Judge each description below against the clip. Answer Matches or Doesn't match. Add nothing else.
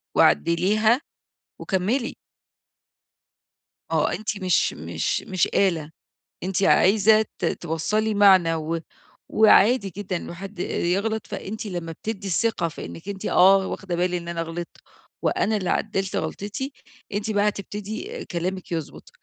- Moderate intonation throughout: Matches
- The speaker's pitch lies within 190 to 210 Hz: Matches